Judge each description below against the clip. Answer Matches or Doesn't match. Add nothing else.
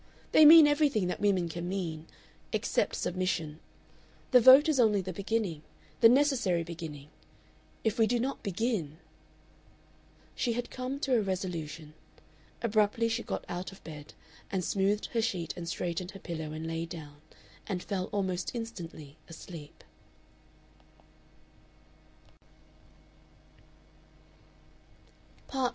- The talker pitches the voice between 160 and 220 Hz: Matches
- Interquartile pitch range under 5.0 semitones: Doesn't match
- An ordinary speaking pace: Doesn't match